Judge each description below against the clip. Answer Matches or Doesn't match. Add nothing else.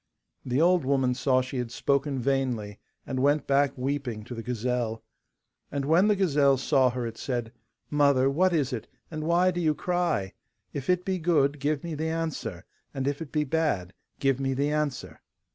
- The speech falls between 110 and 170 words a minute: Doesn't match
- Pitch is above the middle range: Doesn't match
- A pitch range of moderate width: Matches